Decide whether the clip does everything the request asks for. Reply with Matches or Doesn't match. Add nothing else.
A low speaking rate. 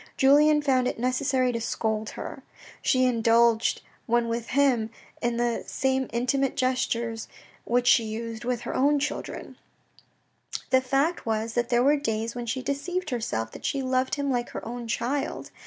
Doesn't match